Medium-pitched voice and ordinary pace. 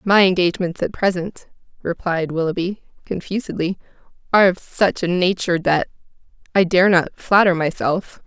No: medium, 180 Hz; slow, 115 wpm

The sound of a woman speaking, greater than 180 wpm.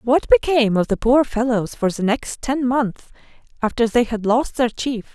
Yes: female; average, 200 wpm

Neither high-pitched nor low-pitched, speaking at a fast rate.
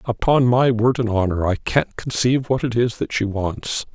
No: low, 115 Hz; fast, 215 wpm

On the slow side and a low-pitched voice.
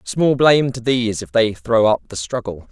No: fast, 220 wpm; low, 115 Hz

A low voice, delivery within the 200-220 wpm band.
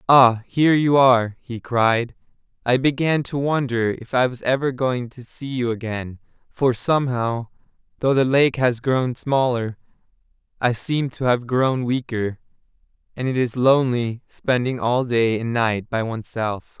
No: low, 125 Hz; average, 155 wpm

